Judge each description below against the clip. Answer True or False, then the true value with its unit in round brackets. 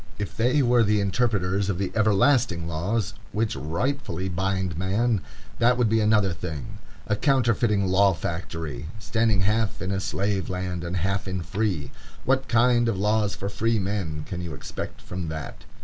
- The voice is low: True (100 Hz)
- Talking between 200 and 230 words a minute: False (170 wpm)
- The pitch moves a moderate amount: True (3.8 semitones)